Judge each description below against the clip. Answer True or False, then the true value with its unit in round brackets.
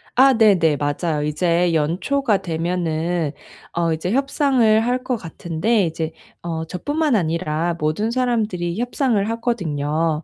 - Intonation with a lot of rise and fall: True (6.2 semitones)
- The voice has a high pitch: False (175 Hz)